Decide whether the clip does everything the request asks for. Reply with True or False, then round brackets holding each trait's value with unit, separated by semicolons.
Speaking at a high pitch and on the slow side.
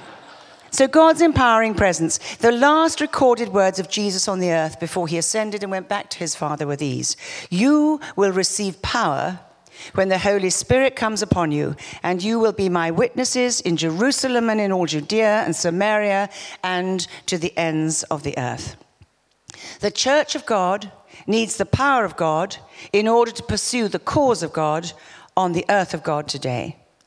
False (195 Hz; 175 wpm)